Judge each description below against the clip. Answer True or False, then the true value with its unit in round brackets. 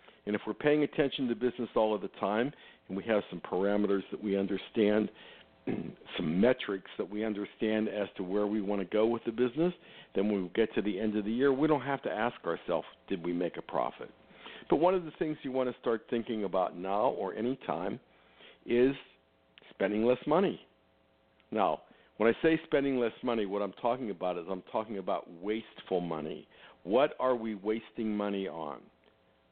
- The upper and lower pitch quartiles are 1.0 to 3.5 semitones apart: False (3.9 semitones)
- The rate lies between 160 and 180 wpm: False (195 wpm)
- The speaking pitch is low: True (105 Hz)